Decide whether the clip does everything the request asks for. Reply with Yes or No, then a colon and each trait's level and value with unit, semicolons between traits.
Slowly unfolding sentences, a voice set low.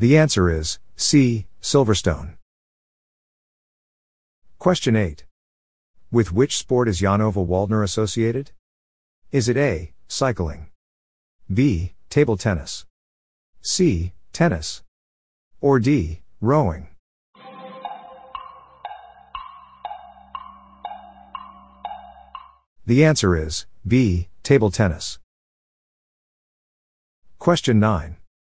Yes: slow, 70 wpm; low, 105 Hz